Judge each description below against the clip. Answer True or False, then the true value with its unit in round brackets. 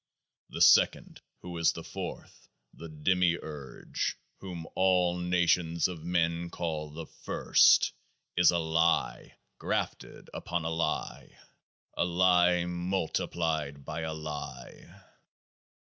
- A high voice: False (85 Hz)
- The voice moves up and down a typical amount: False (1.7 semitones)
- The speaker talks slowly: True (110 wpm)